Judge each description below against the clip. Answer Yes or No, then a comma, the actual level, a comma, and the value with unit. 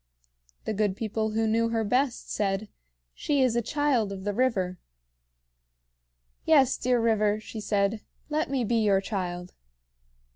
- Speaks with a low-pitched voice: No, high, 220 Hz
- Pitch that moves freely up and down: No, average, 3.2 semitones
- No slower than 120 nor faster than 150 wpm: Yes, average, 145 wpm